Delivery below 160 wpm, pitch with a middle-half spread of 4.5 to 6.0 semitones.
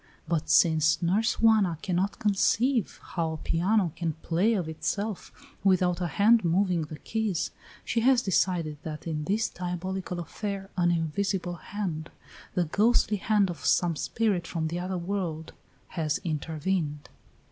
No: average, 145 wpm; average, 3.8 semitones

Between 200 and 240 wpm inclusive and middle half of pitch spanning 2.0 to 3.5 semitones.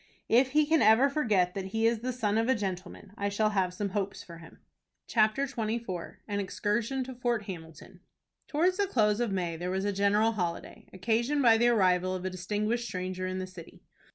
No: fast, 205 wpm; average, 4.1 semitones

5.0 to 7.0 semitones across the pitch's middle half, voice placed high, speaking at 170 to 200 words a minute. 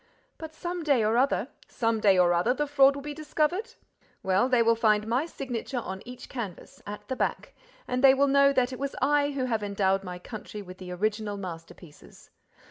Yes: wide, 5.5 semitones; high, 240 Hz; average, 195 wpm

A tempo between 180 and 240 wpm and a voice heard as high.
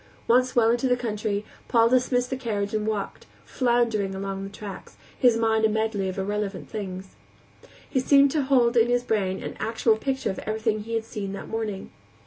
Yes: average, 190 wpm; high, 220 Hz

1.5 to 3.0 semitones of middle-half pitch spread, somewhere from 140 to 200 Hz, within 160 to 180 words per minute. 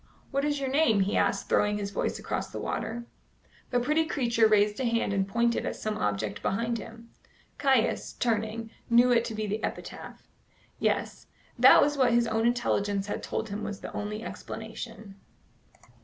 No: narrow, 2.5 semitones; high, 225 Hz; average, 175 wpm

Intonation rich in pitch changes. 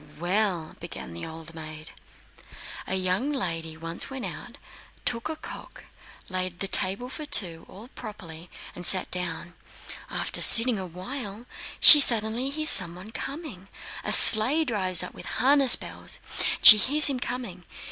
Yes: wide, 6.3 semitones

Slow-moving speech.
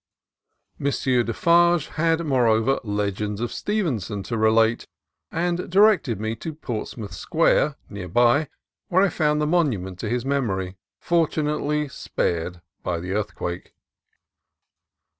Yes: slow, 120 wpm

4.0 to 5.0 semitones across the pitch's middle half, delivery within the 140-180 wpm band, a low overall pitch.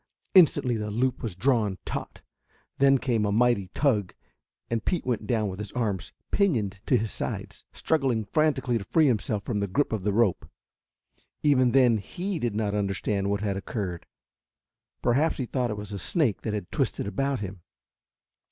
Yes: average, 4.4 semitones; average, 175 wpm; low, 110 Hz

